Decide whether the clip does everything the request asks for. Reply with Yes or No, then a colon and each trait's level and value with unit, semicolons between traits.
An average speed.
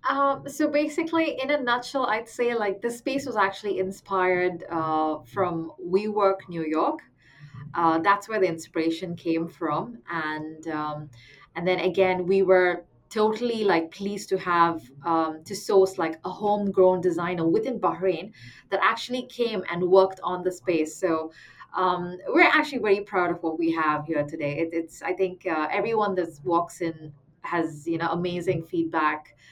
Yes: average, 165 wpm